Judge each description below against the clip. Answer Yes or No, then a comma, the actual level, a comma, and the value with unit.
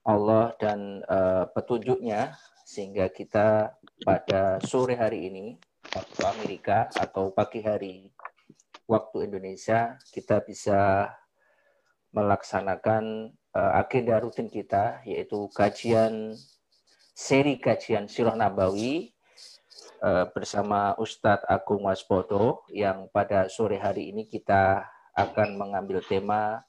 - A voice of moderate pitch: No, low, 105 Hz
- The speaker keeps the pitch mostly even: Yes, narrow, 2.0 semitones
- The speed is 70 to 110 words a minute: Yes, average, 100 wpm